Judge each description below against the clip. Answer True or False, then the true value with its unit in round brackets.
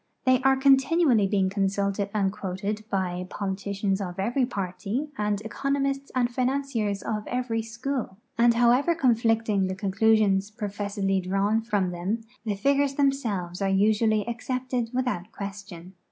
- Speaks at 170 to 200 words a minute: False (135 wpm)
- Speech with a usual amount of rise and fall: True (4.2 semitones)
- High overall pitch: True (215 Hz)